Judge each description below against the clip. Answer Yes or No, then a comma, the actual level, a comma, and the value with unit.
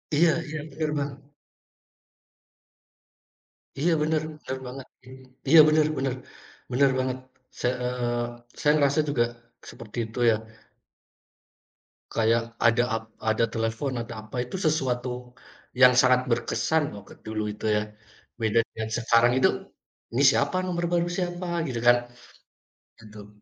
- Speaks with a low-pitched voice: Yes, low, 125 Hz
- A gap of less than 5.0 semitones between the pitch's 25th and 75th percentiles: Yes, average, 4.3 semitones